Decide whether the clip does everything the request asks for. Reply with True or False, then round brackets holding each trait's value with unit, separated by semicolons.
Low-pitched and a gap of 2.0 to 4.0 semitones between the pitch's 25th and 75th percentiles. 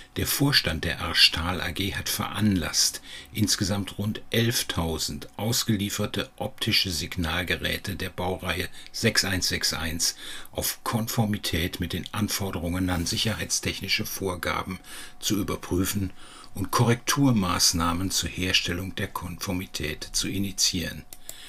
True (95 Hz; 2.8 semitones)